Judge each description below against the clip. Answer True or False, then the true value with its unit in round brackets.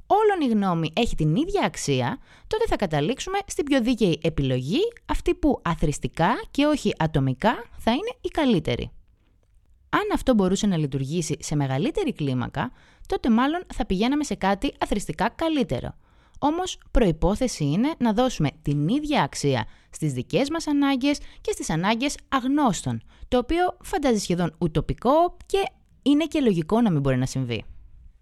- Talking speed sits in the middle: True (150 wpm)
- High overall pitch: True (220 Hz)